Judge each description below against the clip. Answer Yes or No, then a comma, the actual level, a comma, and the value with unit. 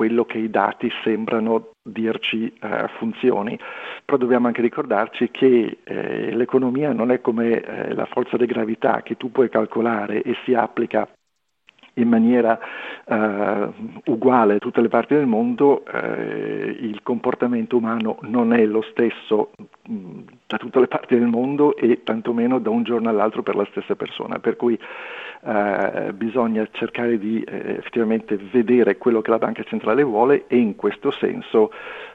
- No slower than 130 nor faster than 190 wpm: Yes, average, 155 wpm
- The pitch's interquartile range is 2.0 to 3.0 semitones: Yes, narrow, 2.4 semitones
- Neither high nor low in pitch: No, low, 120 Hz